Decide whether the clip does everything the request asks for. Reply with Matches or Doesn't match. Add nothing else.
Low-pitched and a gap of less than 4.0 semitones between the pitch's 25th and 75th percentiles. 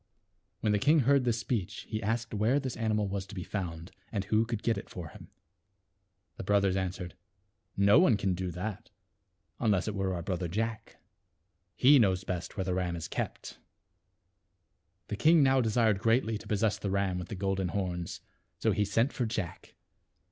Matches